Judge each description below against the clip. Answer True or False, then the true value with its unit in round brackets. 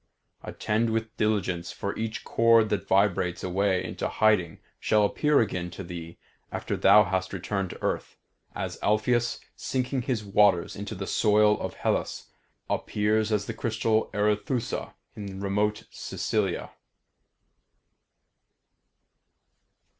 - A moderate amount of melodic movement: False (2.3 semitones)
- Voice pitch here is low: True (105 Hz)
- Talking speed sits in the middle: False (120 wpm)